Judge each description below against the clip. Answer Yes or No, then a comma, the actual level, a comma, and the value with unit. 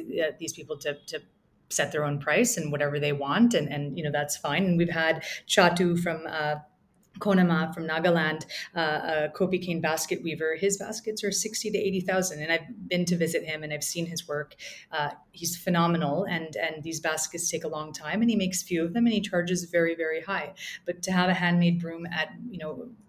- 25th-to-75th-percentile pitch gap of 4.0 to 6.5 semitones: No, average, 3.2 semitones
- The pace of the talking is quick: Yes, fast, 215 wpm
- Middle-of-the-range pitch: Yes, medium, 170 Hz